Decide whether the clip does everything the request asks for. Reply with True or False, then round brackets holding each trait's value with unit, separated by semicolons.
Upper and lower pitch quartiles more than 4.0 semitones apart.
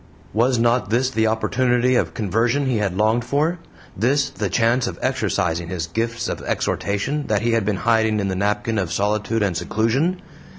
False (3.3 semitones)